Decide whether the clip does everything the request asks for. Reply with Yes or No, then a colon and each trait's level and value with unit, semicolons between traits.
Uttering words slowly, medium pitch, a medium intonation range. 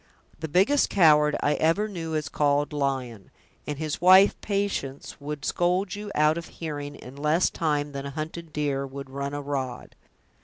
No: average, 175 wpm; medium, 150 Hz; average, 3.1 semitones